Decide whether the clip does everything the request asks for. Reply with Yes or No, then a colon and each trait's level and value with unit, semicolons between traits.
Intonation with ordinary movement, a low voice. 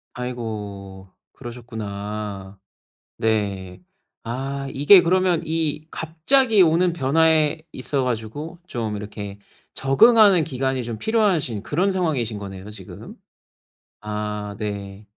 No: wide, 7.4 semitones; low, 125 Hz